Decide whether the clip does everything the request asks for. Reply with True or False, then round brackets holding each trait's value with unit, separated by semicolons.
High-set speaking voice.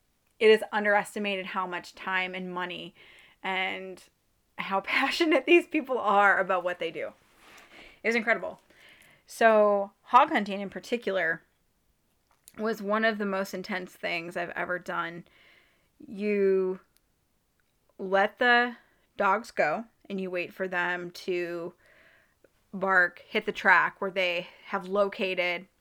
True (195 Hz)